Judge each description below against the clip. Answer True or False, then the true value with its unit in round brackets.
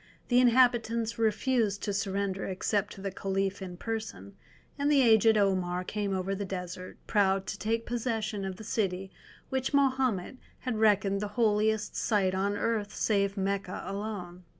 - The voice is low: False (205 Hz)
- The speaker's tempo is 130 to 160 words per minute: True (155 wpm)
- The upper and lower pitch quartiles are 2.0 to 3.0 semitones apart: True (2.7 semitones)